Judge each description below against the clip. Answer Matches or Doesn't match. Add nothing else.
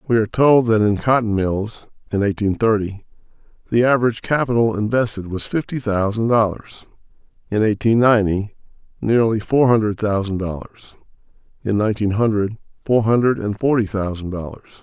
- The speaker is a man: Matches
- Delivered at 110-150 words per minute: Matches